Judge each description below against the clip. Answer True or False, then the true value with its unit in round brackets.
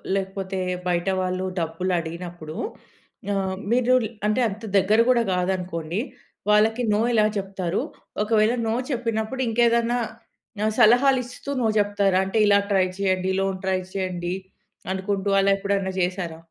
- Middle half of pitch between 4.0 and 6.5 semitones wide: False (3.1 semitones)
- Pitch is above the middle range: True (195 Hz)